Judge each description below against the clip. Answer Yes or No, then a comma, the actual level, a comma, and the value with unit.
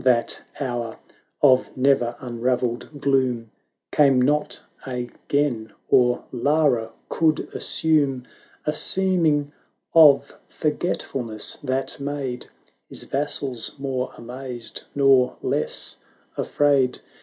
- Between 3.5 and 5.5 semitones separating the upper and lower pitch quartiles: No, average, 2.9 semitones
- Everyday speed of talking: No, slow, 95 wpm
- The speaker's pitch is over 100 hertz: Yes, low, 135 Hz